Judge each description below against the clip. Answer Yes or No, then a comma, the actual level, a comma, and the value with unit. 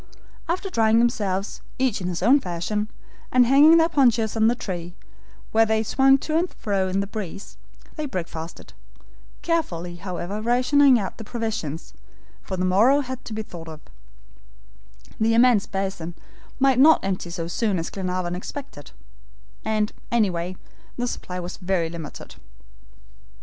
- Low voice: No, high, 210 Hz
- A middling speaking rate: Yes, average, 150 wpm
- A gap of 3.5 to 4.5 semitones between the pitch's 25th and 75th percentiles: No, average, 5.3 semitones